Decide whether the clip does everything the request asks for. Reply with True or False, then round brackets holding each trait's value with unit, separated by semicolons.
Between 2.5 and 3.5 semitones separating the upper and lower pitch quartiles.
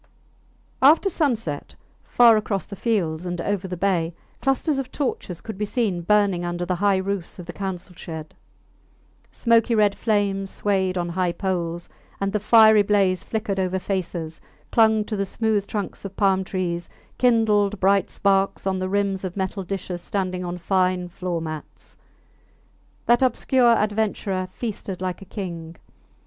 True (2.8 semitones)